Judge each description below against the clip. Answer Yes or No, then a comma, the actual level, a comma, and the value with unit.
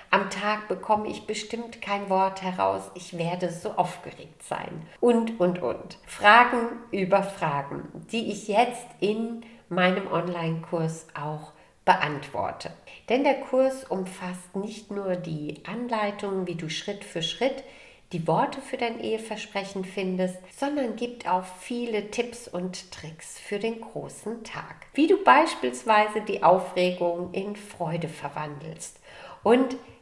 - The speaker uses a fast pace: No, average, 130 wpm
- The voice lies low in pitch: No, high, 195 Hz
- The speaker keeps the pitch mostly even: No, average, 4.5 semitones